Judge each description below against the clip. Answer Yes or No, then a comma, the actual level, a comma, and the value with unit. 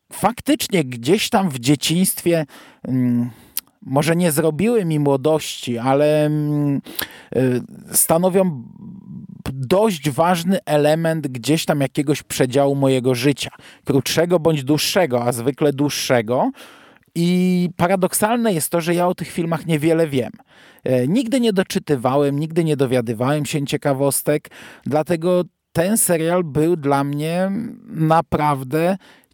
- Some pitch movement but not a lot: Yes, average, 4.2 semitones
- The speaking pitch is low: No, medium, 160 Hz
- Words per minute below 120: Yes, slow, 110 wpm